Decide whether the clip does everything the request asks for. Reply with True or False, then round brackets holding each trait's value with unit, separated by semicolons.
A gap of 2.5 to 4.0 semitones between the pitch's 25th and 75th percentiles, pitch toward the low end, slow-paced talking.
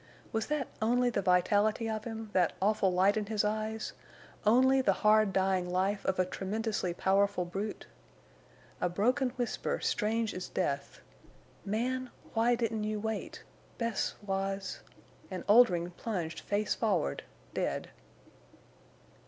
False (2.9 semitones; 210 Hz; 110 wpm)